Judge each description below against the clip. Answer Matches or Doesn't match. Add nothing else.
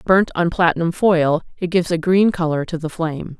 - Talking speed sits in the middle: Doesn't match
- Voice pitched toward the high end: Doesn't match